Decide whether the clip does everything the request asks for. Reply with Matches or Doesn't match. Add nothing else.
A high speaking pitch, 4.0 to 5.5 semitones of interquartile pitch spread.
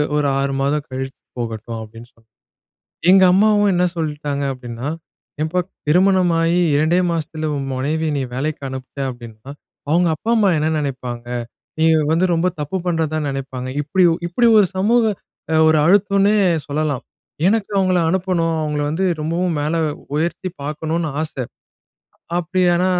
Doesn't match